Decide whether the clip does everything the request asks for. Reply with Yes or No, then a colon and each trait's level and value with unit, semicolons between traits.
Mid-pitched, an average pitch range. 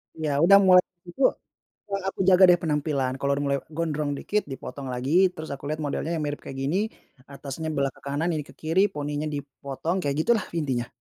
Yes: medium, 150 Hz; average, 3.6 semitones